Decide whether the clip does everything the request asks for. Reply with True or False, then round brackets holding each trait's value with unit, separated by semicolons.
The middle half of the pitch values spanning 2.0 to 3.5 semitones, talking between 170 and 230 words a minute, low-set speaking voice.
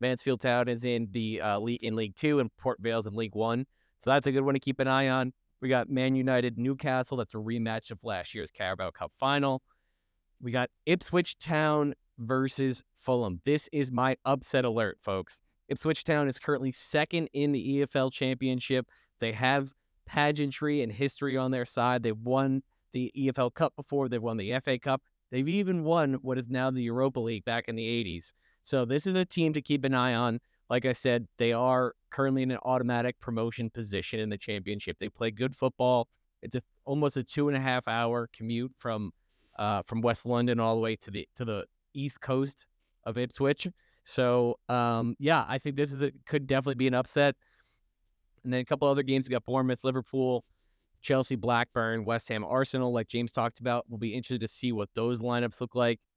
True (2.7 semitones; 200 wpm; 125 Hz)